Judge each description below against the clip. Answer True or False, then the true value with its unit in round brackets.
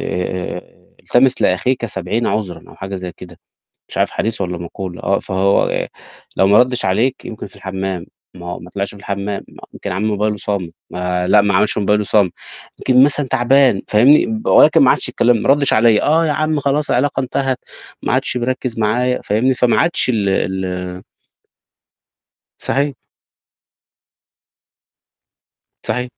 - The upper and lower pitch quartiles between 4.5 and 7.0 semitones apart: True (5.2 semitones)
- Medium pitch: False (105 Hz)